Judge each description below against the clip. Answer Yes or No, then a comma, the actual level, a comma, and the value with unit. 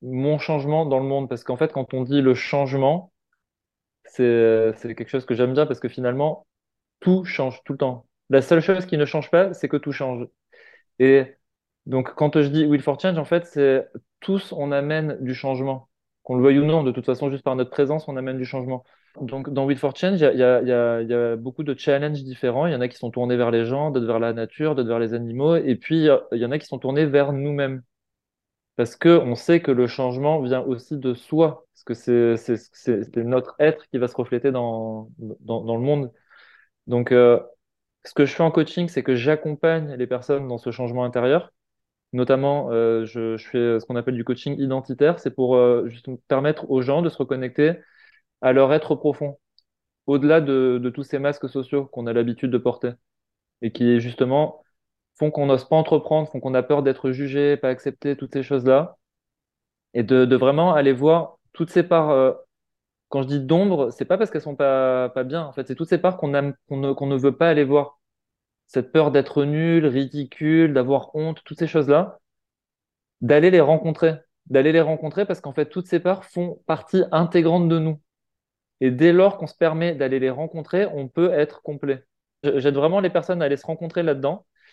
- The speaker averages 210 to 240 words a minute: Yes, average, 215 wpm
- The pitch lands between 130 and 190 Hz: Yes, medium, 140 Hz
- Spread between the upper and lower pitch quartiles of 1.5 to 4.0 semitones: Yes, average, 3.7 semitones